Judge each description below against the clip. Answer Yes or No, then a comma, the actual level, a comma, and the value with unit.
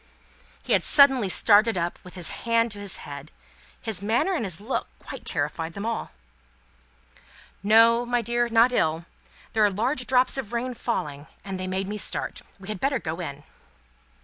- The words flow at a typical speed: Yes, average, 175 wpm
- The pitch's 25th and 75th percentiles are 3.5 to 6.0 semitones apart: Yes, average, 4.4 semitones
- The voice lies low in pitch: No, high, 215 Hz